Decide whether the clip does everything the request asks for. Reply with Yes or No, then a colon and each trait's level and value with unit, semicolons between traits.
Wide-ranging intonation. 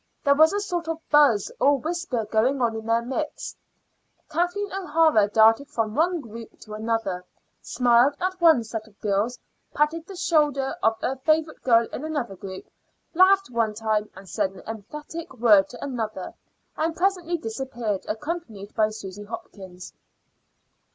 Yes: wide, 6.5 semitones